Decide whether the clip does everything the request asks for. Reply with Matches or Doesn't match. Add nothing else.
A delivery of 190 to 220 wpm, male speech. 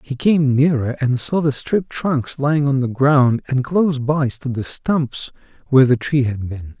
Matches